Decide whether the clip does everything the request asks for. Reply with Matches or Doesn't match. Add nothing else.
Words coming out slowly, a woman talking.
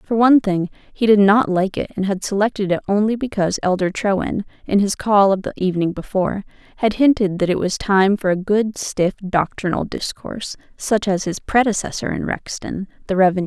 Doesn't match